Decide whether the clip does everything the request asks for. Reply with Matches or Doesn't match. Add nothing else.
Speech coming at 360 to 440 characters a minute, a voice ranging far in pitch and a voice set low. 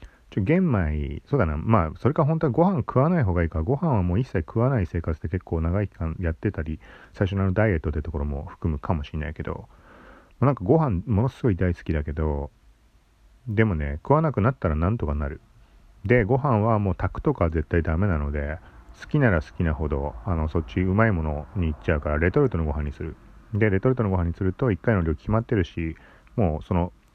Matches